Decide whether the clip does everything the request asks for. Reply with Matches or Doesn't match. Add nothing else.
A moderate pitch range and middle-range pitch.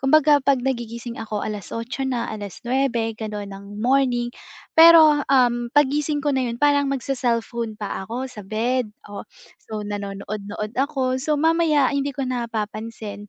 Doesn't match